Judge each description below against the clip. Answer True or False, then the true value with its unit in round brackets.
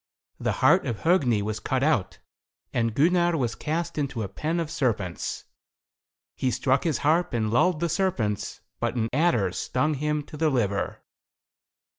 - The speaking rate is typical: True (160 wpm)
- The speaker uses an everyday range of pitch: False (6.0 semitones)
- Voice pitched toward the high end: False (140 Hz)